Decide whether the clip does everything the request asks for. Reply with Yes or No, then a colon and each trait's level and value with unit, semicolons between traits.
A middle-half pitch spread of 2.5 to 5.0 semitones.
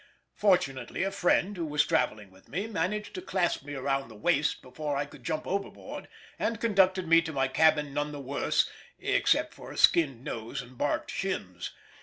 No: wide, 5.4 semitones